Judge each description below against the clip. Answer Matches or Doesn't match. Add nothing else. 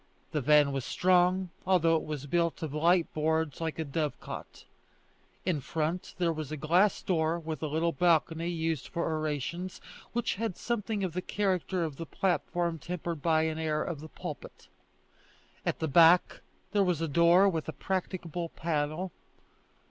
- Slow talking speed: Doesn't match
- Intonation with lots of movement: Doesn't match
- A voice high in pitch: Doesn't match